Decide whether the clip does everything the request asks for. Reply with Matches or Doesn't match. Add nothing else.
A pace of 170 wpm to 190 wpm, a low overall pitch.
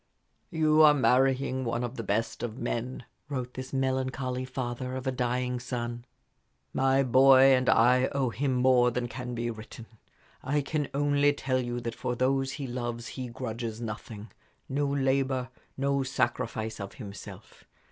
Doesn't match